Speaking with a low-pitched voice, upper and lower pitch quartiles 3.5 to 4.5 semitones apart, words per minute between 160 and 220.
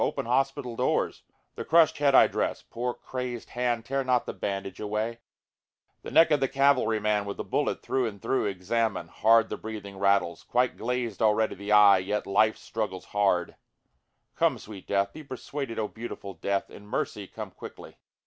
Yes: low, 110 Hz; average, 3.8 semitones; average, 175 wpm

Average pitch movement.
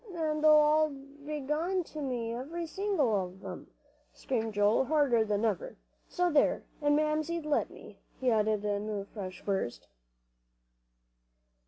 No: wide, 6.2 semitones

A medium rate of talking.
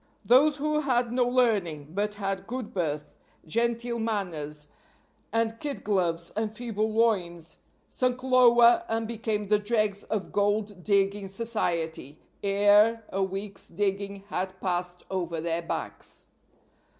No: slow, 125 wpm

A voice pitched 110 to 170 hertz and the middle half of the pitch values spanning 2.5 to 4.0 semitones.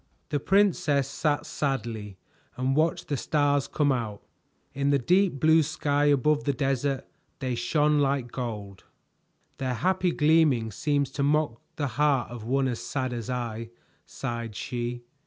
Yes: low, 135 Hz; average, 3.5 semitones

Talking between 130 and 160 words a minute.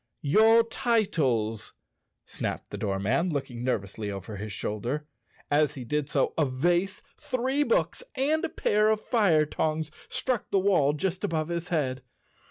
Yes: average, 155 wpm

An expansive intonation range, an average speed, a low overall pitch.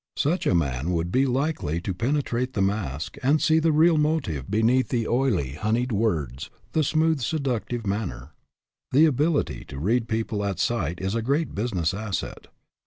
Yes: wide, 7.5 semitones; average, 170 wpm; low, 115 Hz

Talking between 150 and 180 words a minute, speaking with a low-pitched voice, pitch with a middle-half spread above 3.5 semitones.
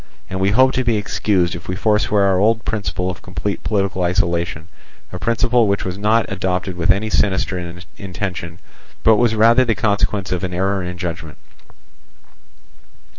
No: average, 165 wpm; very low, 95 Hz; average, 3.1 semitones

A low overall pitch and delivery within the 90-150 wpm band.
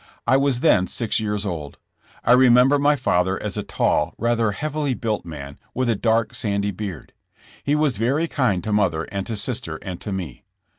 No: low, 110 Hz; average, 190 wpm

